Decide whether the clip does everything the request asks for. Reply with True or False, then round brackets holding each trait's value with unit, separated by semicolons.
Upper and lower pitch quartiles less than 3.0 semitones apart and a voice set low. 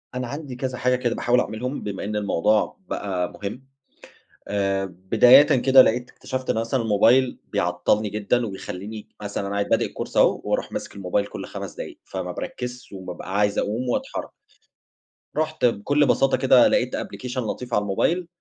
False (4.0 semitones; 115 Hz)